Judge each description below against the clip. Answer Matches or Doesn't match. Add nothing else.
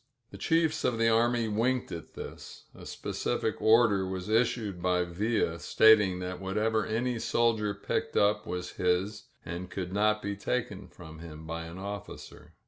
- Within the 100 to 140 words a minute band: Doesn't match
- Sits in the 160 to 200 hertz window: Doesn't match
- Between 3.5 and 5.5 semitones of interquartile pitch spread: Matches